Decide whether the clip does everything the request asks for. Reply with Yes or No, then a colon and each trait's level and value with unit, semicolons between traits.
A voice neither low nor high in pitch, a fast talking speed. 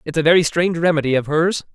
Yes: medium, 160 Hz; fast, 240 wpm